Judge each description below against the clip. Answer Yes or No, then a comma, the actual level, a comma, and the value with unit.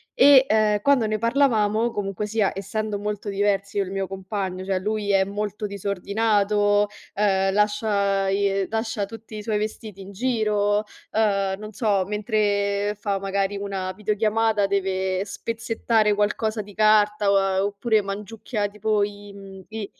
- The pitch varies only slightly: Yes, narrow, 1.5 semitones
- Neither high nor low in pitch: No, high, 205 Hz